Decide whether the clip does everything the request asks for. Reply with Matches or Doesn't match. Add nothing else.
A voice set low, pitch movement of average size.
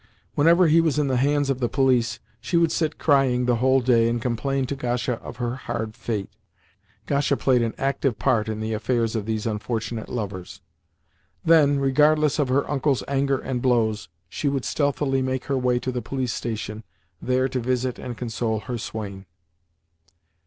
Matches